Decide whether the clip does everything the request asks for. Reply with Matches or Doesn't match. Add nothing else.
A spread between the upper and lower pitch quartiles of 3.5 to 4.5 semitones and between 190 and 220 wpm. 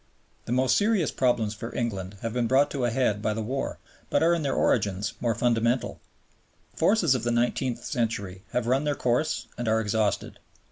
Doesn't match